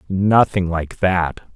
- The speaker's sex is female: No, male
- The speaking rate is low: Yes, slow, 115 wpm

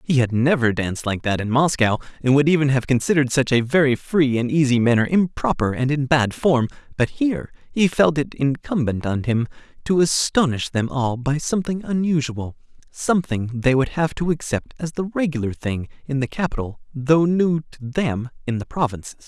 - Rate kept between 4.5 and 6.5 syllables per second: Yes, 5.3 syllables/s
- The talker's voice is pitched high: No, medium, 140 Hz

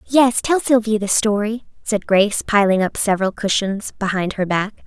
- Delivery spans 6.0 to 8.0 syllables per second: No, 5.1 syllables/s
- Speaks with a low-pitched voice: No, high, 210 Hz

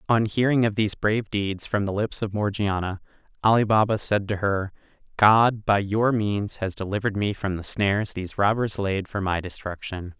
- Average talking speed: Yes, average, 190 wpm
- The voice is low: Yes, low, 100 Hz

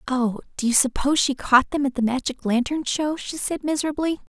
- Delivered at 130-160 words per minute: No, fast, 205 wpm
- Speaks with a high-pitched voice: Yes, very high, 270 Hz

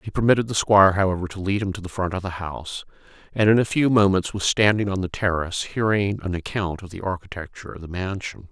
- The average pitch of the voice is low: Yes, very low, 95 Hz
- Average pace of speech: No, fast, 230 wpm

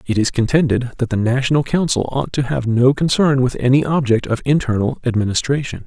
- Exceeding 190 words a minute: No, average, 185 wpm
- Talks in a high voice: No, low, 130 Hz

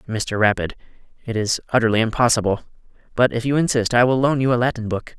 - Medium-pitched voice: No, low, 120 Hz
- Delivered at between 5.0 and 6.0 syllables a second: No, 6.4 syllables/s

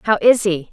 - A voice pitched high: Yes, high, 200 Hz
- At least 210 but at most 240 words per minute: No, fast, 250 wpm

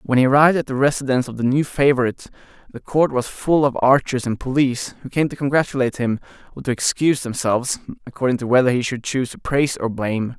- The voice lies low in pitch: Yes, low, 130 Hz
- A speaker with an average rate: No, fast, 215 wpm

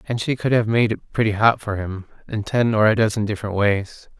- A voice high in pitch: No, low, 110 Hz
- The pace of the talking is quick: Yes, fast, 245 wpm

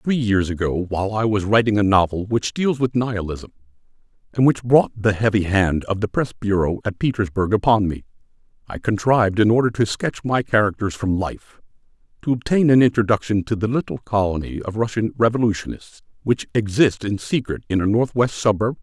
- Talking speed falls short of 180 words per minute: No, average, 185 wpm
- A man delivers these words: Yes, male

